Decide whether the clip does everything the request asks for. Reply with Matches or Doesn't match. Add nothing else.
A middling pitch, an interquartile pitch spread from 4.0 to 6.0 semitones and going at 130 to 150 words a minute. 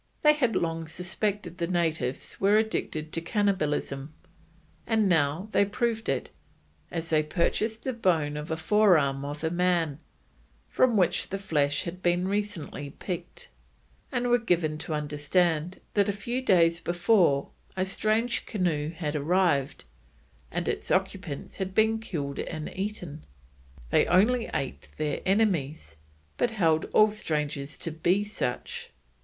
Matches